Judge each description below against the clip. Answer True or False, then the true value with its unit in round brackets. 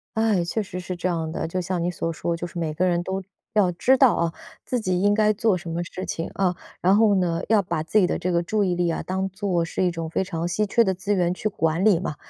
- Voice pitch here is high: False (180 Hz)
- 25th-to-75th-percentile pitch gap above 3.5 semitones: False (2.9 semitones)